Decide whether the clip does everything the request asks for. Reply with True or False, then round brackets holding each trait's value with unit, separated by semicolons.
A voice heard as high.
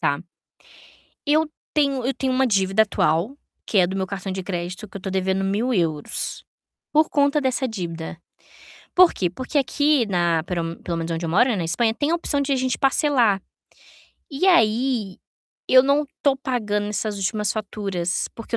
True (215 Hz)